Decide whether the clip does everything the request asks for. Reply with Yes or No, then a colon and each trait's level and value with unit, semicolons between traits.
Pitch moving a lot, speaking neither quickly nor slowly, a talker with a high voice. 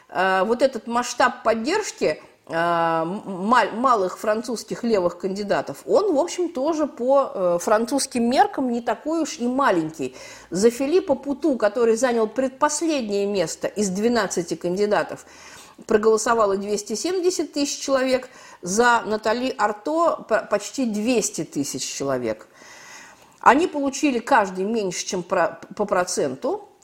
No: wide, 6.5 semitones; slow, 105 wpm; high, 230 Hz